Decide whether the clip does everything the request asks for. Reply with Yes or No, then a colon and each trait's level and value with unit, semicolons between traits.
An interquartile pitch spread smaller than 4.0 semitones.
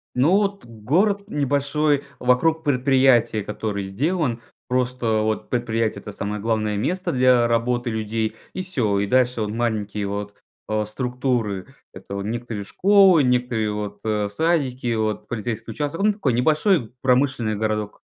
No: average, 4.5 semitones